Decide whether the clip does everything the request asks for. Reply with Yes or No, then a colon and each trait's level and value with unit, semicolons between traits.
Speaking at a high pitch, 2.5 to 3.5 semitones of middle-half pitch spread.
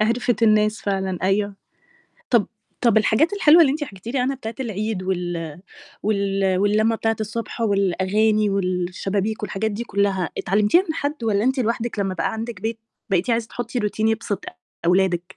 Yes: high, 210 Hz; average, 3.0 semitones